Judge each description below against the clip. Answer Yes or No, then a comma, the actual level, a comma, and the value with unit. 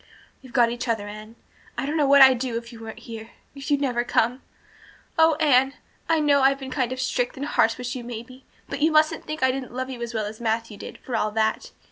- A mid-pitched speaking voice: No, very high, 250 Hz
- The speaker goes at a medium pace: No, fast, 245 wpm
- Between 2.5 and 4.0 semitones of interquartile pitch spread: Yes, average, 2.9 semitones